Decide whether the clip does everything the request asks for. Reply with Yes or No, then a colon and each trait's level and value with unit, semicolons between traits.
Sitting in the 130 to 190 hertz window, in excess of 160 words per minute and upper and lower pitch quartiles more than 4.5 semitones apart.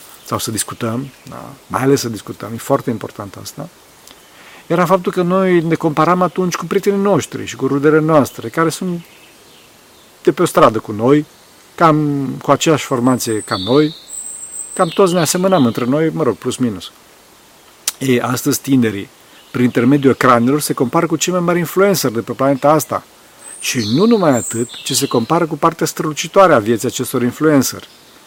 Yes: medium, 140 Hz; fast, 170 wpm; average, 5.2 semitones